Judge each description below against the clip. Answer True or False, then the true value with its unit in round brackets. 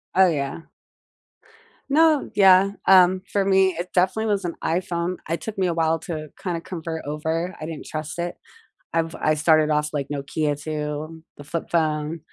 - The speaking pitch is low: False (165 Hz)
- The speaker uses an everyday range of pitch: True (3.1 semitones)